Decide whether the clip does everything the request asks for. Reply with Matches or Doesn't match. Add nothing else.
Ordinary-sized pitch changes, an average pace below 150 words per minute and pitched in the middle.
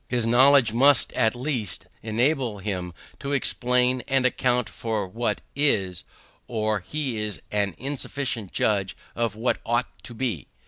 Doesn't match